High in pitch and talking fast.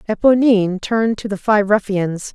No: high, 210 Hz; average, 155 wpm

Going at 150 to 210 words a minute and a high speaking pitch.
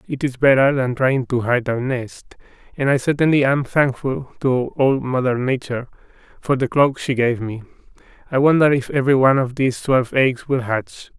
No: average, 190 wpm; low, 130 Hz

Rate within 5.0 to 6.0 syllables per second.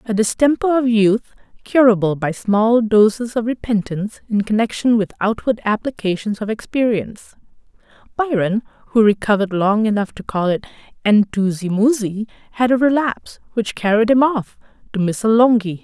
Yes: 5.2 syllables/s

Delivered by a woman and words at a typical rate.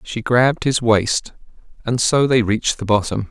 No: male; average, 180 wpm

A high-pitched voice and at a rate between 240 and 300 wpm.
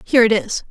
Yes: high, 230 Hz; fast, 255 wpm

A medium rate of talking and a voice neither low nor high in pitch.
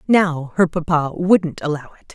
Yes: average, 170 wpm; medium, 165 Hz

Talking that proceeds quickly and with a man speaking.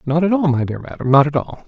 Yes: fast, 325 wpm; male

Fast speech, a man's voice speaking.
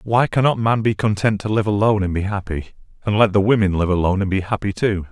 Yes: fast, 245 wpm; male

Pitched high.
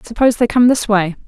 Yes: high, 225 Hz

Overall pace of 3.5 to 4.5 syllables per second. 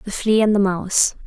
No: 5.6 syllables/s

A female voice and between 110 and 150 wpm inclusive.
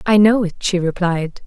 No: female; fast, 205 wpm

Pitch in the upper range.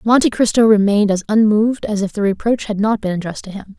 Yes: high, 210 Hz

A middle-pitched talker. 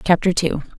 Yes: medium, 170 Hz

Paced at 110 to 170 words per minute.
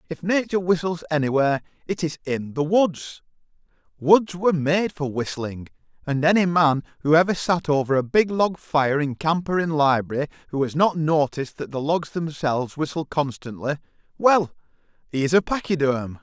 Yes: average, 165 wpm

